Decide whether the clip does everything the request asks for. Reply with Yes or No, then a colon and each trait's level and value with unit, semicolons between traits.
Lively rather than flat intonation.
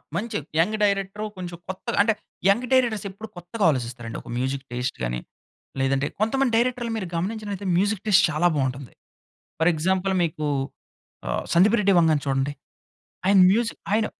Yes: wide, 6.8 semitones